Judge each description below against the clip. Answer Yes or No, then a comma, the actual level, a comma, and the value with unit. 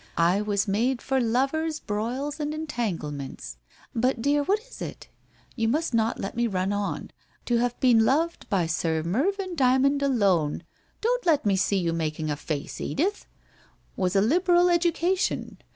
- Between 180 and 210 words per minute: No, average, 170 wpm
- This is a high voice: Yes, high, 240 Hz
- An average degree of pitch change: No, wide, 7.8 semitones